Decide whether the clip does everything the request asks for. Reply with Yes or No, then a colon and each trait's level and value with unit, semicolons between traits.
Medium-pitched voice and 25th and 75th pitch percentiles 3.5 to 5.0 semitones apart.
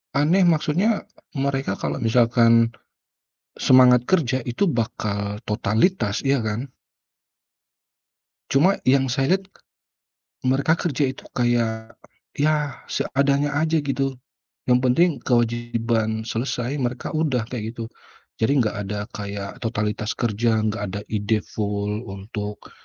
No: low, 120 Hz; average, 4.0 semitones